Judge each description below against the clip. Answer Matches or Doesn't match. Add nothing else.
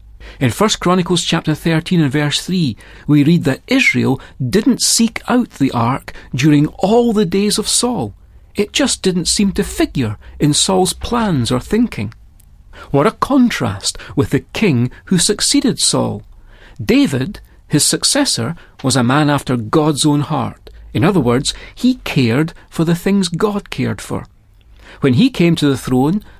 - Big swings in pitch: Matches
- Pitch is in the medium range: Matches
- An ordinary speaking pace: Matches